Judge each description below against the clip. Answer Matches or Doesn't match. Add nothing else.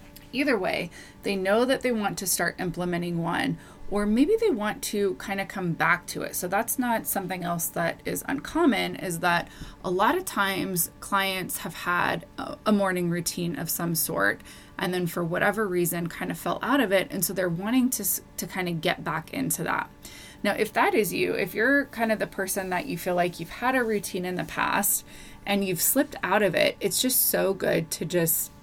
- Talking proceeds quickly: Matches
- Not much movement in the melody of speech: Doesn't match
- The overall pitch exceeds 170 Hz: Matches